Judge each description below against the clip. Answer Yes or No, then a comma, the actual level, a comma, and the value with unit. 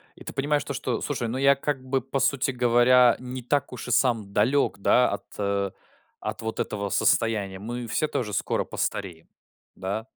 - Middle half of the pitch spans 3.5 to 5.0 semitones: Yes, average, 4.1 semitones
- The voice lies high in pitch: No, low, 120 Hz